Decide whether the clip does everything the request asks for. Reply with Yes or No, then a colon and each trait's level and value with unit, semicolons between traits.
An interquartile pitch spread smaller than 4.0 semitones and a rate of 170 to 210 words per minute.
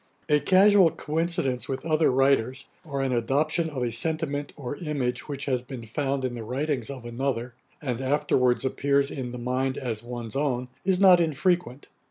Yes: average, 3.5 semitones; average, 175 wpm